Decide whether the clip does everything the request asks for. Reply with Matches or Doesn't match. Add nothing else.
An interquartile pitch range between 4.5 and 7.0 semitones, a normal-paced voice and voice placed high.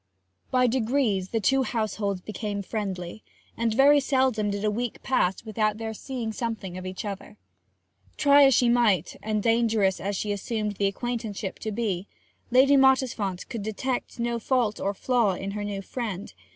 Doesn't match